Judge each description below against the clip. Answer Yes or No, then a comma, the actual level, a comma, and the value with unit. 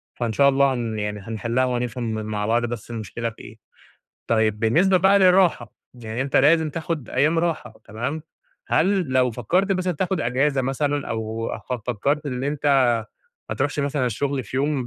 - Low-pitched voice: Yes, low, 130 Hz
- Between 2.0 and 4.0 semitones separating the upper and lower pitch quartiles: No, average, 4.7 semitones